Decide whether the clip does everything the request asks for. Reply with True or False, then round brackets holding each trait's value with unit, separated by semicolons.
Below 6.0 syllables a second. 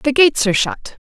False (6.3 syllables/s)